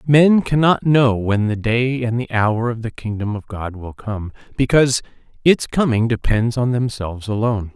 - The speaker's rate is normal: Yes, average, 180 wpm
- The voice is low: Yes, low, 115 Hz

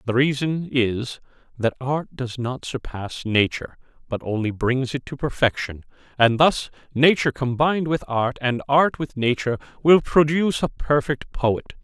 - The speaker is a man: Yes, male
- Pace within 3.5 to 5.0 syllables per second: Yes, 4.7 syllables/s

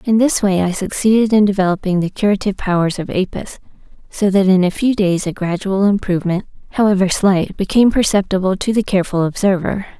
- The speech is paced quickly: No, average, 175 wpm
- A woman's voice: Yes, female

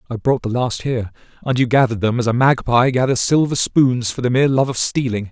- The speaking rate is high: Yes, fast, 225 wpm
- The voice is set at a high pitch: No, low, 125 Hz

